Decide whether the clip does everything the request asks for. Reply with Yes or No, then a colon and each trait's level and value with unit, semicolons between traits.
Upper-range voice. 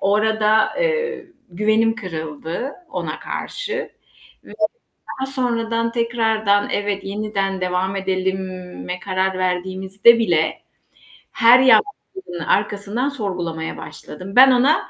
Yes: high, 205 Hz